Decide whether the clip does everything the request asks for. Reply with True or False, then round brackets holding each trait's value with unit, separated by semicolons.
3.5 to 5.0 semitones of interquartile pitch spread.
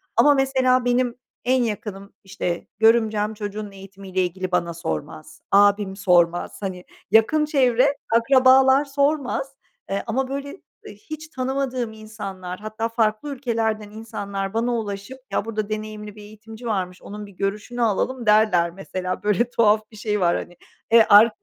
True (3.9 semitones)